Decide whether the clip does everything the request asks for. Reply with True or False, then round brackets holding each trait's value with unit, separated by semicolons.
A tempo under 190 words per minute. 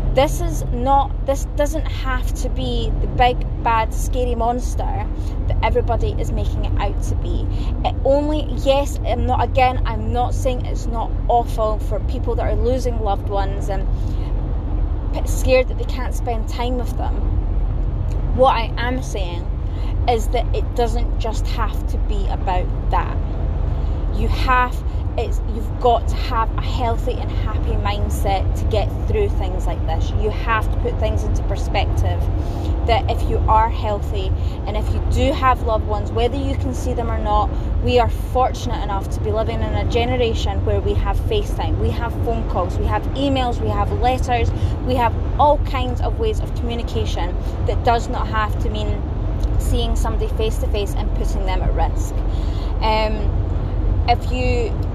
True (175 wpm)